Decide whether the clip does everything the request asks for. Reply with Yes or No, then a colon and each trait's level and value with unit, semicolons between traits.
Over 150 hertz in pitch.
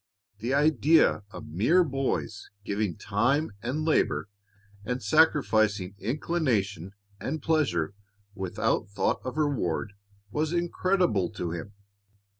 No: low, 125 Hz